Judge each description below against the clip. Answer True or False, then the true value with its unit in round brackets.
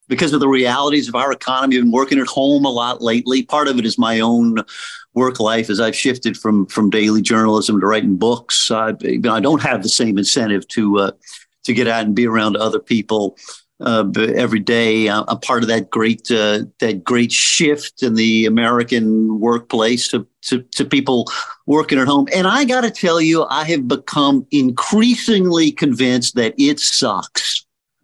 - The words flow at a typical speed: True (185 wpm)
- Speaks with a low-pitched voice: True (120 Hz)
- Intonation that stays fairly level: False (3.9 semitones)